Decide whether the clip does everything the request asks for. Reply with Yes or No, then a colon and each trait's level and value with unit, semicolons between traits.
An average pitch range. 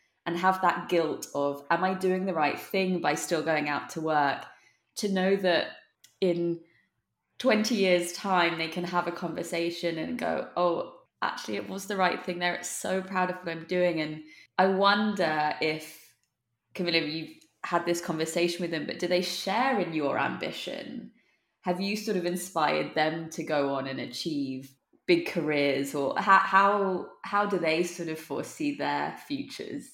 Yes: average, 3.1 semitones